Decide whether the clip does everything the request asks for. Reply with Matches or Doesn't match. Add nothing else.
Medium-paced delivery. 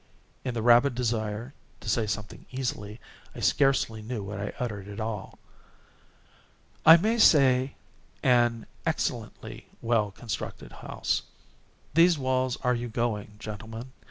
Doesn't match